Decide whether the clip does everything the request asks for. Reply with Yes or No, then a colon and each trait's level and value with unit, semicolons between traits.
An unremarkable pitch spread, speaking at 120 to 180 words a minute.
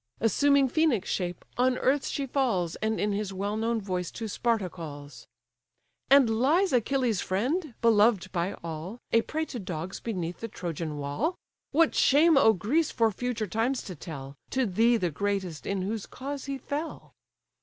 No: wide, 6.3 semitones; average, 165 wpm